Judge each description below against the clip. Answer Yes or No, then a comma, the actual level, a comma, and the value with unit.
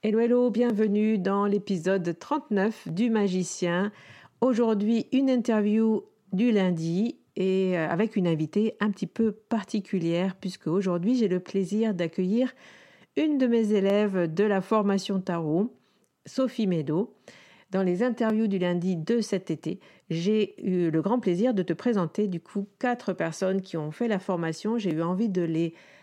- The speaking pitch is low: No, high, 200 Hz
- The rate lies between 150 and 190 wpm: Yes, average, 155 wpm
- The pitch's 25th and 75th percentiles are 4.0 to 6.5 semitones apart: No, average, 3.6 semitones